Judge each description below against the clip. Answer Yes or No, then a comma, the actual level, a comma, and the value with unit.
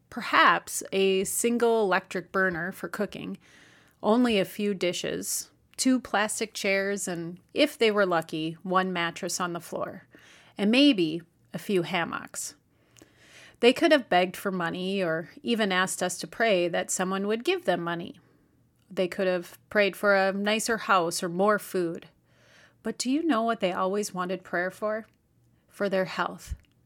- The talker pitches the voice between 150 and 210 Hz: Yes, high, 190 Hz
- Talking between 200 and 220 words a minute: No, average, 160 wpm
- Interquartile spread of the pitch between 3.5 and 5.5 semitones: No, average, 3.0 semitones